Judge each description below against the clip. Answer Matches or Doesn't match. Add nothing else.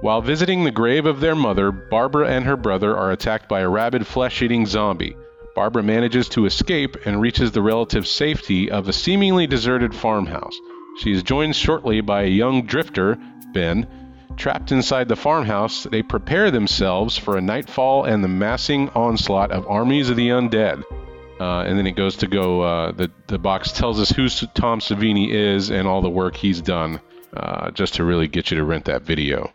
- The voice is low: Matches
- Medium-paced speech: Matches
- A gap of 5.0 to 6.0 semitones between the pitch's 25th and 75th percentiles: Matches